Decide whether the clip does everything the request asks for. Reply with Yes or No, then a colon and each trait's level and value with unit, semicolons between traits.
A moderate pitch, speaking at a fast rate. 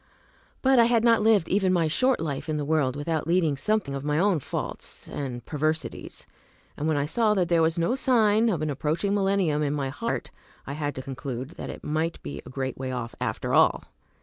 Yes: medium, 155 Hz; fast, 215 wpm